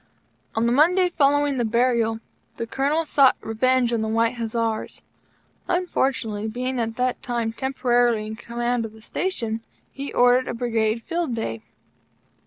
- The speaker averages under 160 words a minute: Yes, average, 150 wpm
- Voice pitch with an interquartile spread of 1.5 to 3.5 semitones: Yes, average, 2.9 semitones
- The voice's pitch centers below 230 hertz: No, high, 240 Hz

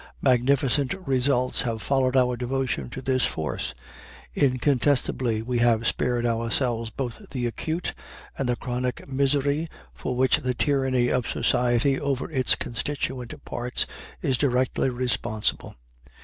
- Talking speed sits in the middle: No, slow, 125 wpm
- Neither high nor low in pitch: No, low, 125 Hz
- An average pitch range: No, narrow, 2.0 semitones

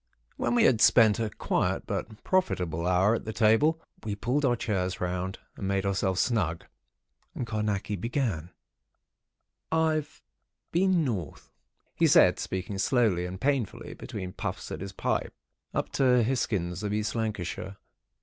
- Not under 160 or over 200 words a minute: No, average, 145 wpm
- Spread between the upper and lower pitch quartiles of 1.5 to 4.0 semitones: No, average, 4.6 semitones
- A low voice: Yes, low, 105 Hz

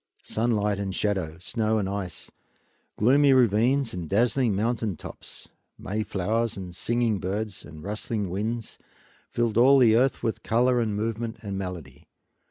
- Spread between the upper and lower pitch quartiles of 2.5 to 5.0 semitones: Yes, average, 3.3 semitones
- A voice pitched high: No, low, 110 Hz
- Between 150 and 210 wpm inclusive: No, average, 140 wpm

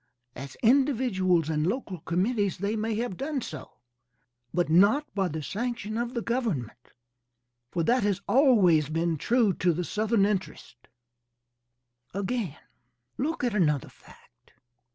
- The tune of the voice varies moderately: No, wide, 5.9 semitones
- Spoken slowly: Yes, slow, 130 wpm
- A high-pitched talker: Yes, high, 200 Hz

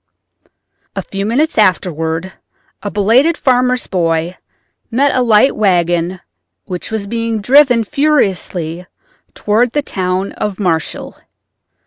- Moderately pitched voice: No, high, 205 Hz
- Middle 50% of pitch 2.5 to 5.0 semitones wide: No, wide, 5.4 semitones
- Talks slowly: Yes, slow, 110 wpm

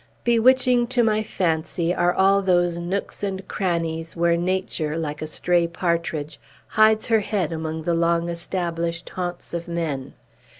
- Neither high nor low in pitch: Yes, medium, 170 Hz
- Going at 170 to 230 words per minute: No, average, 145 wpm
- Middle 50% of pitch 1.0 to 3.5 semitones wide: Yes, average, 2.7 semitones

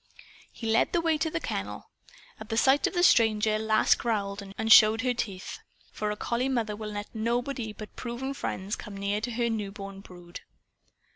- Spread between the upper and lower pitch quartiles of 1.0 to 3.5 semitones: Yes, average, 2.7 semitones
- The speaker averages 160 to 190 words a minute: Yes, average, 185 wpm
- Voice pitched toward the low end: No, high, 220 Hz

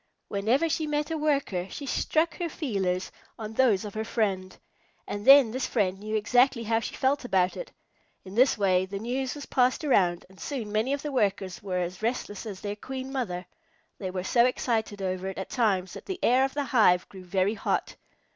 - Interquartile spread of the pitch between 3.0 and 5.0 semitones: No, wide, 5.6 semitones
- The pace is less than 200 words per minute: No, fast, 205 wpm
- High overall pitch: Yes, high, 220 Hz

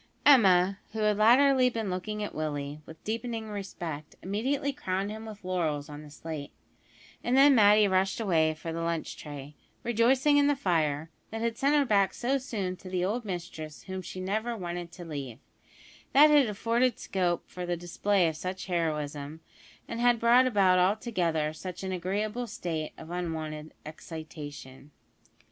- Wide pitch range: Yes, wide, 5.7 semitones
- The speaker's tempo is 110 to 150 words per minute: No, average, 165 wpm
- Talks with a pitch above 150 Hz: Yes, medium, 185 Hz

